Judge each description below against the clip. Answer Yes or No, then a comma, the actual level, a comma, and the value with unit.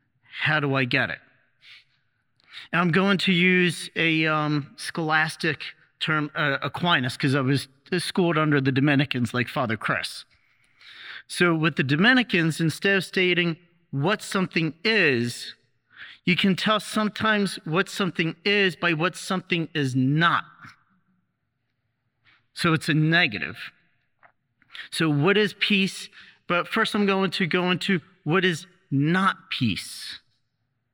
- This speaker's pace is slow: Yes, slow, 130 wpm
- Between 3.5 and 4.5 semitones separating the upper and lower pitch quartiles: No, average, 5.0 semitones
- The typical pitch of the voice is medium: Yes, medium, 165 Hz